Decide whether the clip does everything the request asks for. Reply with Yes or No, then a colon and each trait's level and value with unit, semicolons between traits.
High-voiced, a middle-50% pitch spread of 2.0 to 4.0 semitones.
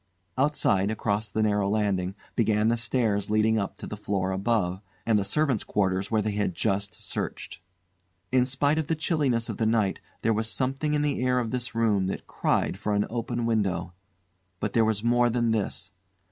No: low, 110 Hz; average, 3.1 semitones